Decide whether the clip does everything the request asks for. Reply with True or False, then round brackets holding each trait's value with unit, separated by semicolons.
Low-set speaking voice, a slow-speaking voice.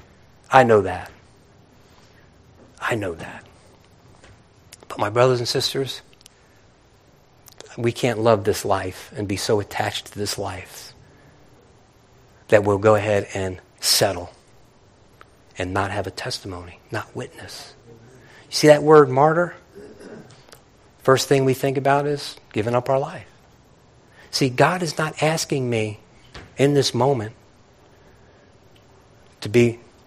True (120 Hz; 125 wpm)